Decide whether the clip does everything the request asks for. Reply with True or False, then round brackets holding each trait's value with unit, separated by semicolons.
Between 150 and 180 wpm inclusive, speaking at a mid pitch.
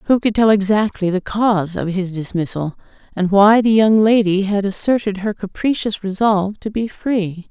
False (175 wpm; 200 Hz)